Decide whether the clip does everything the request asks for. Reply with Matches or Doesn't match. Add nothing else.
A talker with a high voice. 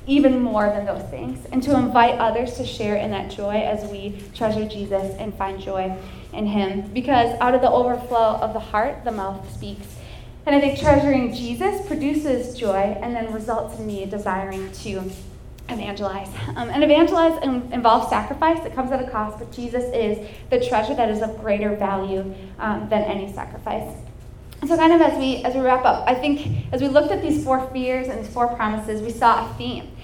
Matches